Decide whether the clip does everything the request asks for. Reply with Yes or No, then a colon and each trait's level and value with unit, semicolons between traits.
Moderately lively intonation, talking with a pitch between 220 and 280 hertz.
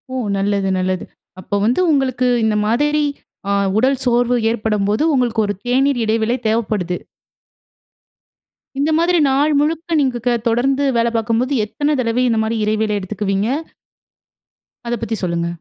Yes: average, 4.0 semitones; high, 230 Hz